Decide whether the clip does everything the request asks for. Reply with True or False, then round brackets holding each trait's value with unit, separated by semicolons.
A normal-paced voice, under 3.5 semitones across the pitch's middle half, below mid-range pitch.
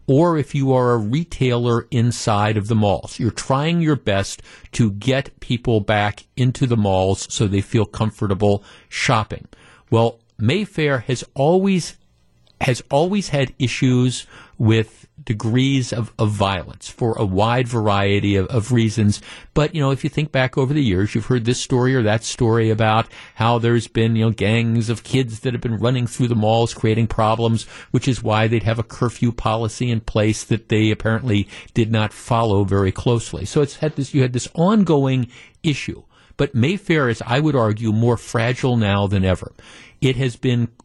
True (180 wpm; 3.1 semitones; 115 Hz)